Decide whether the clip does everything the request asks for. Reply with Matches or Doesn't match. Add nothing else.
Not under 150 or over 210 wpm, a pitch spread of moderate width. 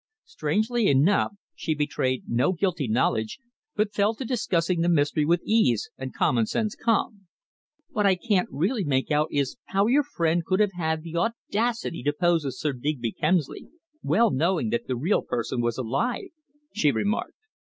Doesn't match